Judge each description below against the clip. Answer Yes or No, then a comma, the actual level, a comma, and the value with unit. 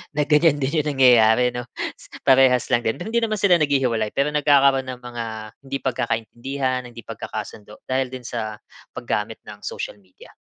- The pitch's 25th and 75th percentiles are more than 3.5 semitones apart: No, average, 3.1 semitones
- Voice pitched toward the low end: Yes, low, 130 Hz